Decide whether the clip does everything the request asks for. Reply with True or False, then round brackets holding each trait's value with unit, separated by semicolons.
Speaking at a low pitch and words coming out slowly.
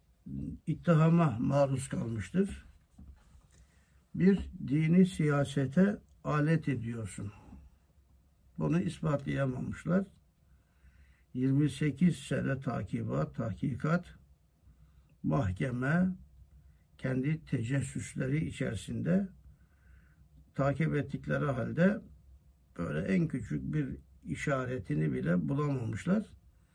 True (130 Hz; 65 wpm)